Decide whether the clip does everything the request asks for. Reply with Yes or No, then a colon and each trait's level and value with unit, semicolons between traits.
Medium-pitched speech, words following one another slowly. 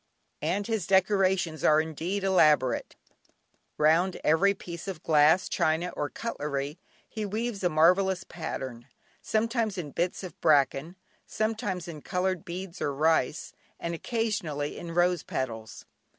Yes: medium, 175 Hz; slow, 130 wpm